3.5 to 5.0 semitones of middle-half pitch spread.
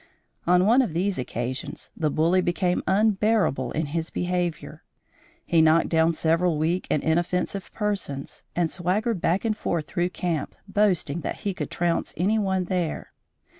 No: average, 3.1 semitones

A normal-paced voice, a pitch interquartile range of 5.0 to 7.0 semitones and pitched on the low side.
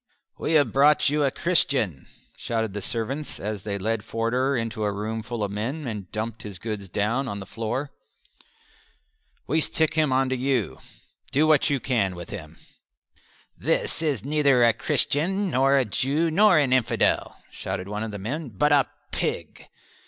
Yes: average, 175 wpm; average, 5.3 semitones; low, 125 Hz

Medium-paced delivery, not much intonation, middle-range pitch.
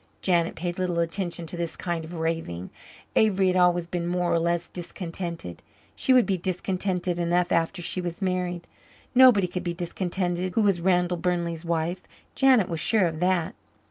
Yes: average, 175 wpm; narrow, 1.5 semitones; medium, 175 Hz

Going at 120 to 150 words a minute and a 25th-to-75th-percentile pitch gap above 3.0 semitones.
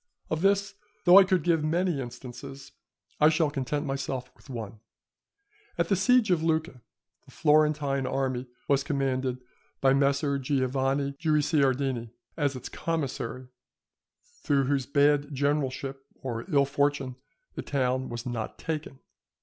No: slow, 135 wpm; average, 2.7 semitones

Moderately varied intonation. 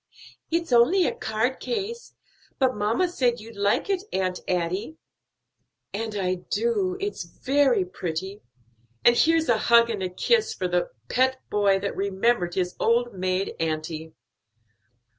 No: wide, 6.9 semitones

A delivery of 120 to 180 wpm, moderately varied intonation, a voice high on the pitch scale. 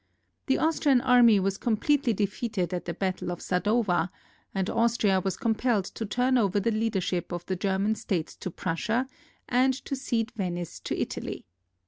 Yes: average, 165 wpm; average, 4.4 semitones; high, 210 Hz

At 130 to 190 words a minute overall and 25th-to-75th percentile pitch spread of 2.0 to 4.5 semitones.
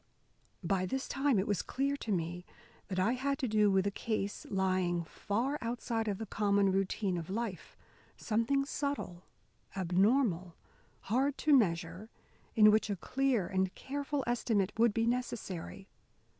No: average, 150 wpm; average, 4.9 semitones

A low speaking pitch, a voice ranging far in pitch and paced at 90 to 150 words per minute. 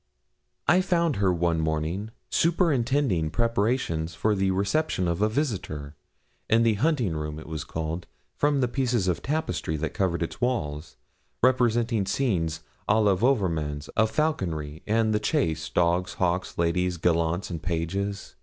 Yes: very low, 95 Hz; wide, 6.4 semitones; average, 145 wpm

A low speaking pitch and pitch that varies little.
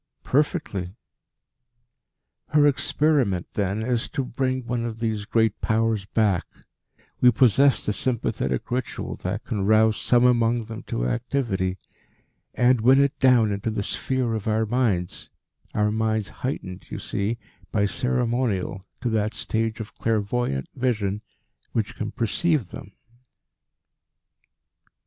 No: low, 115 Hz; average, 3.2 semitones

